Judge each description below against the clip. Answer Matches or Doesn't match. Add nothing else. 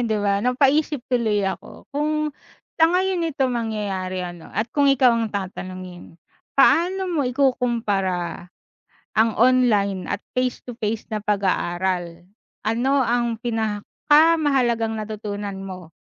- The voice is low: Doesn't match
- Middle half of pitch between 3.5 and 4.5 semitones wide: Doesn't match